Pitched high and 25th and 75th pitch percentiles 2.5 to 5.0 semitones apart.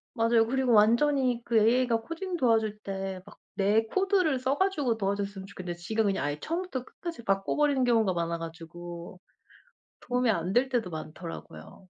No: high, 225 Hz; wide, 5.4 semitones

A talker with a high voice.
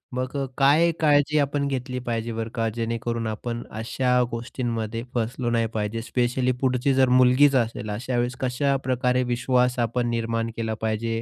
No: low, 125 Hz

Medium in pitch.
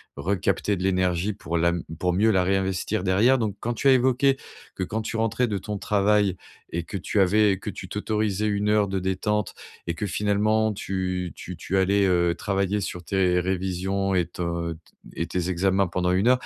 No: very low, 95 Hz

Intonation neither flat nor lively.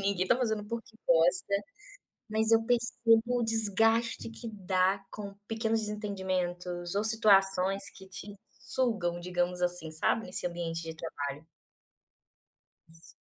Yes: average, 4.0 semitones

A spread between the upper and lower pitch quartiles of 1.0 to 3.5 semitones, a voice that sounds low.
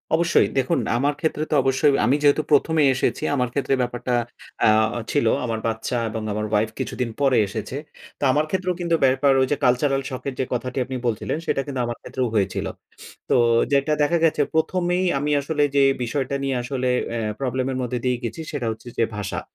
Yes: average, 3.2 semitones; low, 130 Hz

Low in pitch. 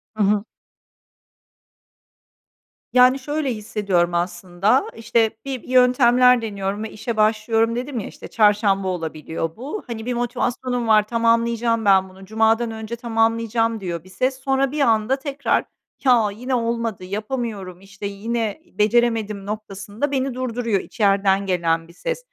No: high, 225 Hz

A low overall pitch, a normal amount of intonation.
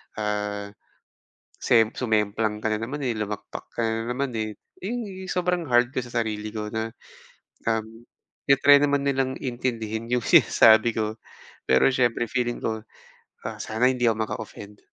Yes: low, 115 Hz; average, 3.1 semitones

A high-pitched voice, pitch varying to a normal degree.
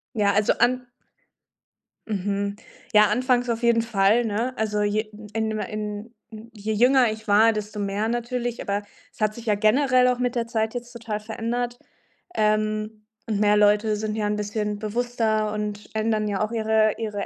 No: high, 215 Hz; narrow, 2.0 semitones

